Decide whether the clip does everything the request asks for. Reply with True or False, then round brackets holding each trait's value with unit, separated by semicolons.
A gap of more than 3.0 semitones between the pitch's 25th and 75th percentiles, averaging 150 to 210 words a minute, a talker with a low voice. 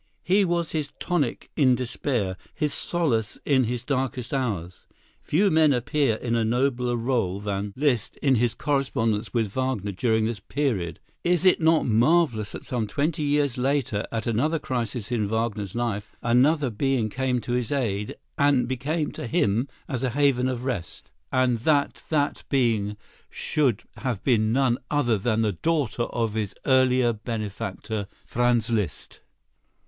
True (4.1 semitones; 155 wpm; 125 Hz)